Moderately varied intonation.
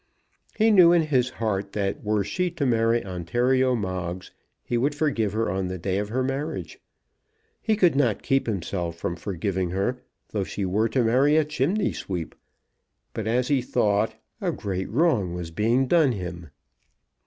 No: wide, 5.8 semitones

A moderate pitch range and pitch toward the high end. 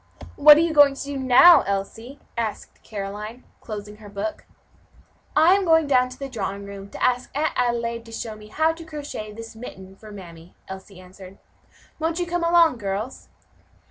No: wide, 6.7 semitones; high, 235 Hz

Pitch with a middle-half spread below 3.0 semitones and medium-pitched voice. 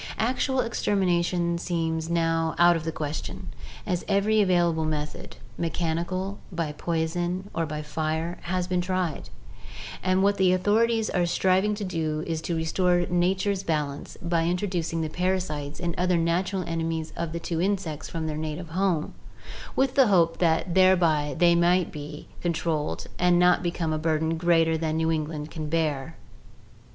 Yes: narrow, 2.4 semitones; medium, 170 Hz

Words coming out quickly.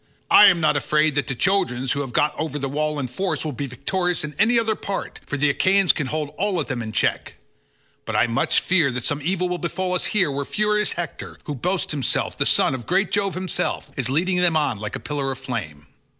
Yes: fast, 235 wpm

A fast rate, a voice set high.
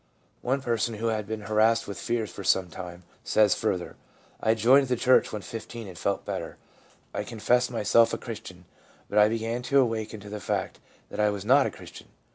No: fast, 210 wpm; low, 110 Hz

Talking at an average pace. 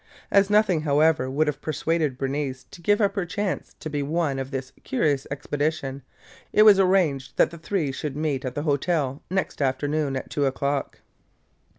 Yes: average, 180 wpm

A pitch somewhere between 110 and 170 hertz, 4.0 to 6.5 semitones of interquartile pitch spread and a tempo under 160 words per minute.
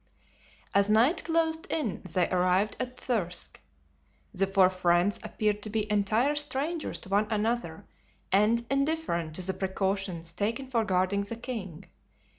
No: high, 210 Hz; average, 4.6 semitones; average, 140 wpm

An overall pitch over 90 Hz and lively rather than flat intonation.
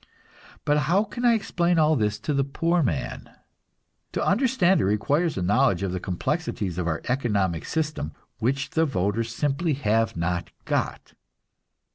Yes: low, 135 Hz; wide, 8.6 semitones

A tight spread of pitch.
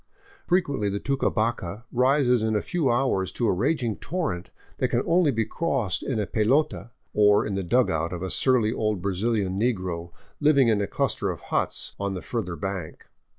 No: average, 5.3 semitones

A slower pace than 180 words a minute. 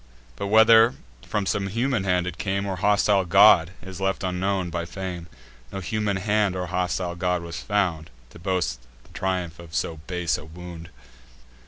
Yes: average, 170 wpm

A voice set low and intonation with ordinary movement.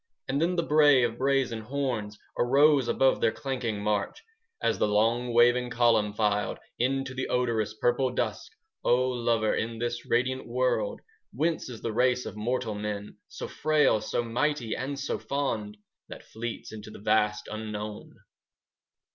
Yes: low, 120 Hz; average, 3.3 semitones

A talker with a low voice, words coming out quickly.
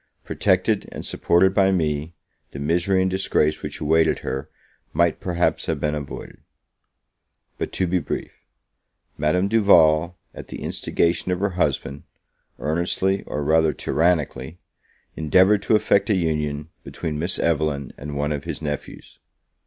No: very low, 80 Hz; average, 140 wpm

